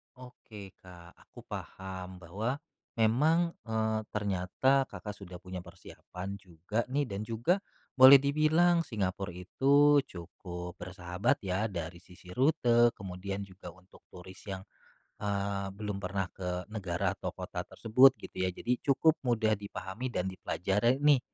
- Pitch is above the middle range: No, low, 100 Hz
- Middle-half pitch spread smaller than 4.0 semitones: No, average, 5.2 semitones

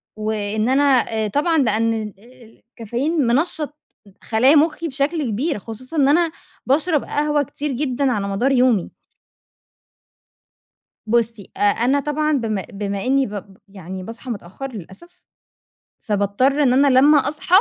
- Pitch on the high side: Yes, very high, 255 Hz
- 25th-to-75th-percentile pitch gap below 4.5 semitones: No, average, 5.2 semitones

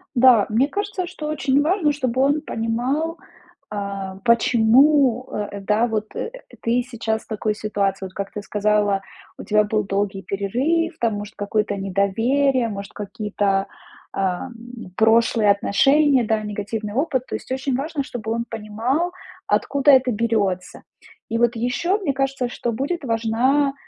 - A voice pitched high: Yes, high, 230 Hz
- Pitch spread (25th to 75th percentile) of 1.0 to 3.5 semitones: No, average, 4.7 semitones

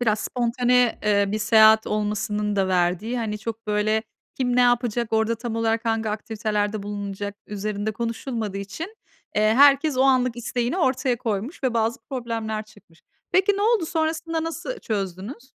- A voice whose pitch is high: Yes, high, 225 Hz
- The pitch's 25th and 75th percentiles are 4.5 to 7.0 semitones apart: No, average, 3.1 semitones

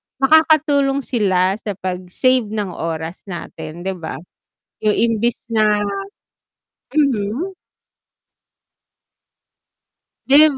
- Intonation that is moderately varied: No, wide, 6.6 semitones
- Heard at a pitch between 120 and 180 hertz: No, high, 215 Hz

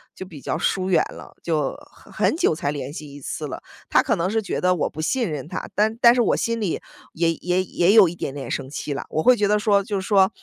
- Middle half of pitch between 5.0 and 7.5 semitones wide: Yes, average, 5.3 semitones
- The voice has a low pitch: No, medium, 185 Hz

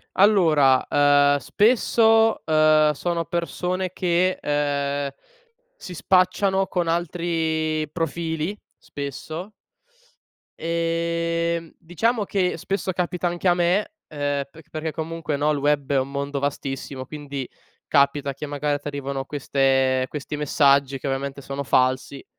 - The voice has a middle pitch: Yes, medium, 155 Hz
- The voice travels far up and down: No, average, 3.6 semitones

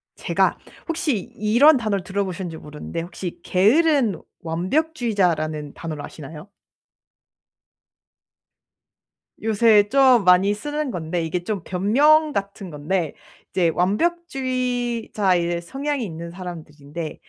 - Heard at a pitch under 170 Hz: No, high, 195 Hz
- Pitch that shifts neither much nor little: No, wide, 6.8 semitones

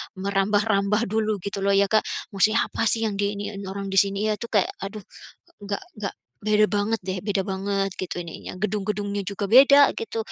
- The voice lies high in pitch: Yes, high, 205 Hz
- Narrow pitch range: Yes, narrow, 1.4 semitones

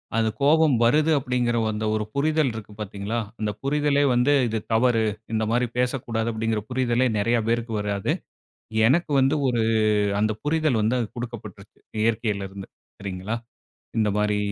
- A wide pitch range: No, average, 3.3 semitones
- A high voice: No, low, 115 Hz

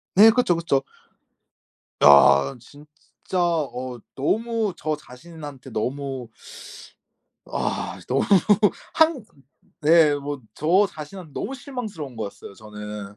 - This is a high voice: No, medium, 150 Hz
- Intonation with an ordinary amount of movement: No, wide, 6.4 semitones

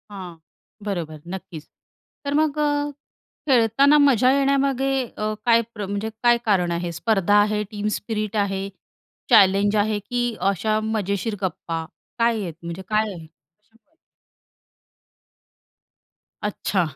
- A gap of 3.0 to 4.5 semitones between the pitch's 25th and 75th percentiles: Yes, average, 3.5 semitones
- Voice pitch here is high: Yes, high, 210 Hz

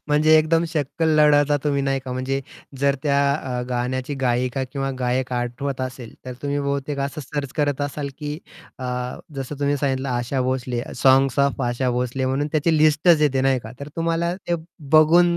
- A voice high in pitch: No, medium, 140 Hz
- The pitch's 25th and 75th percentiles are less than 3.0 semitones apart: Yes, narrow, 2.4 semitones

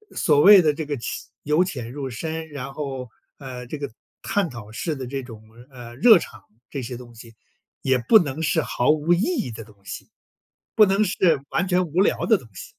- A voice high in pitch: No, medium, 145 Hz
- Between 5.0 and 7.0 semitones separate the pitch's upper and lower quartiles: Yes, wide, 5.4 semitones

